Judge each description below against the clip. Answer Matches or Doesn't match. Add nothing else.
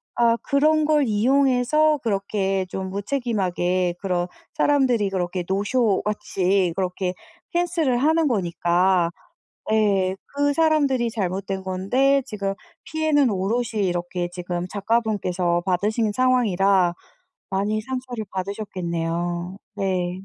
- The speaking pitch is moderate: Doesn't match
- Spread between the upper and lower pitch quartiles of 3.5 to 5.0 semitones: Doesn't match